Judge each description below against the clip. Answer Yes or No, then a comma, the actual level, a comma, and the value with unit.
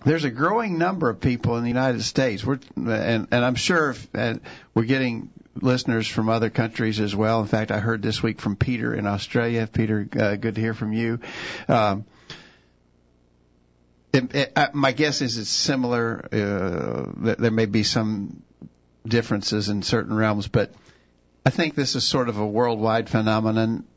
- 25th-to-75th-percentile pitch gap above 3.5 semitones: No, average, 2.9 semitones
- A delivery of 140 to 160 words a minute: No, average, 180 wpm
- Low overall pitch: Yes, low, 115 Hz